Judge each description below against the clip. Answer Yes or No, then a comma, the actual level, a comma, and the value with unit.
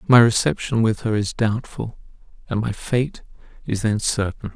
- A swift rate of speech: No, average, 160 wpm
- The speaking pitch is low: Yes, low, 110 Hz